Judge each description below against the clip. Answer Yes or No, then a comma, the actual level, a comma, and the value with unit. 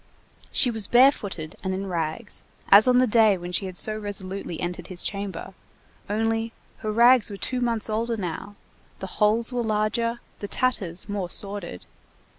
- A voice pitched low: No, high, 210 Hz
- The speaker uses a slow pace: No, average, 165 wpm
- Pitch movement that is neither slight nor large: Yes, average, 3.4 semitones